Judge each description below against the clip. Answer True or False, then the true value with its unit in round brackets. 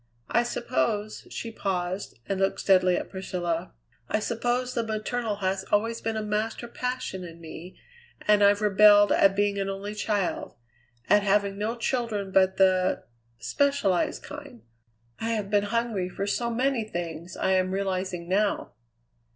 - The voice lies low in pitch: False (205 Hz)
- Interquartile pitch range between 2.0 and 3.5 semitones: True (3.2 semitones)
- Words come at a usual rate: True (150 wpm)